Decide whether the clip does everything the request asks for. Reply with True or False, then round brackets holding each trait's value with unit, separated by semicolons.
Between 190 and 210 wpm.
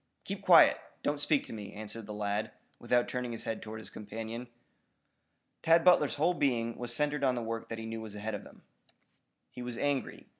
True (200 wpm)